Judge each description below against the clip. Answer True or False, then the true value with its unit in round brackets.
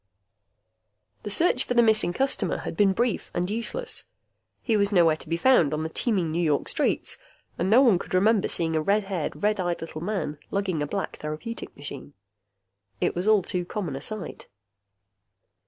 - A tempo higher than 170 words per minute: True (185 wpm)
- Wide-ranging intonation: False (4.8 semitones)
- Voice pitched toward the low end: False (190 Hz)